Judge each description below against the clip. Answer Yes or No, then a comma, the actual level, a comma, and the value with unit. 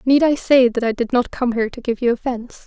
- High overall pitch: Yes, high, 245 Hz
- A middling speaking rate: No, fast, 290 wpm